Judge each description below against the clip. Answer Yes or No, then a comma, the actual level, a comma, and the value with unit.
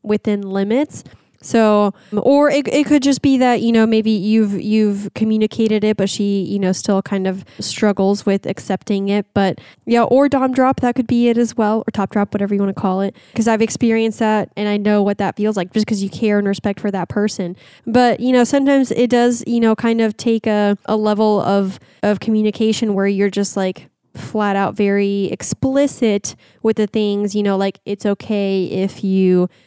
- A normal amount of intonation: No, narrow, 2.3 semitones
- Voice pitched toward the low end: No, high, 210 Hz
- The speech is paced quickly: Yes, fast, 210 wpm